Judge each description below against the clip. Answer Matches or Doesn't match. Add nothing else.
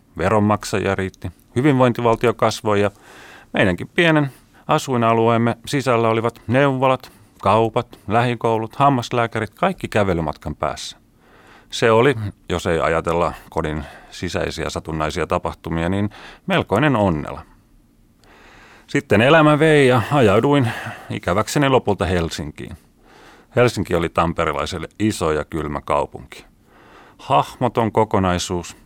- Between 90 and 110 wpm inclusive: Matches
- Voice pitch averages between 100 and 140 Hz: Matches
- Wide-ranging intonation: Matches